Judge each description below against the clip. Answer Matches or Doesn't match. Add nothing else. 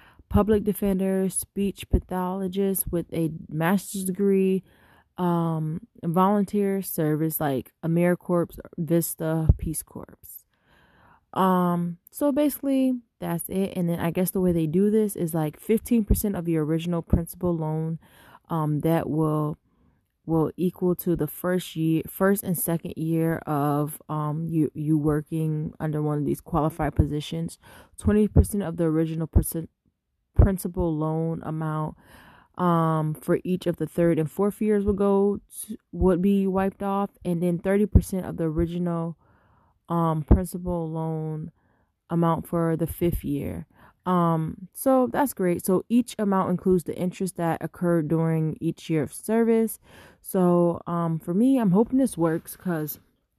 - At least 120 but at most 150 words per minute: Matches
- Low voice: Doesn't match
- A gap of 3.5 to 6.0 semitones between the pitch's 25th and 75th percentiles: Doesn't match